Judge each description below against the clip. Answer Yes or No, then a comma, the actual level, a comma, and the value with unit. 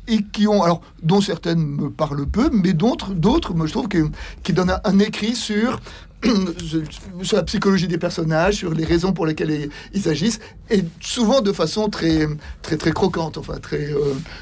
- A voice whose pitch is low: No, medium, 175 Hz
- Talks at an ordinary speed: Yes, average, 185 wpm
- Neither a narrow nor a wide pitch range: Yes, average, 4.4 semitones